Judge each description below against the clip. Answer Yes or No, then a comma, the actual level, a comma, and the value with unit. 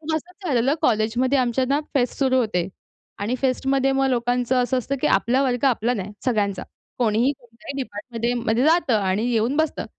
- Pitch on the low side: No, high, 245 Hz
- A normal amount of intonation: Yes, average, 3.1 semitones